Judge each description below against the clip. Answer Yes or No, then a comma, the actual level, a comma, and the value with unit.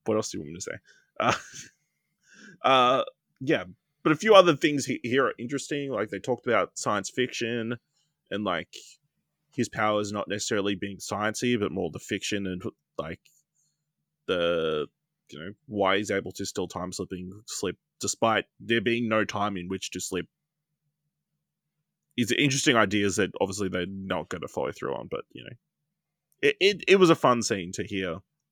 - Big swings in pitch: Yes, wide, 7.6 semitones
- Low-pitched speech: Yes, low, 115 Hz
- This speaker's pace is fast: No, average, 175 wpm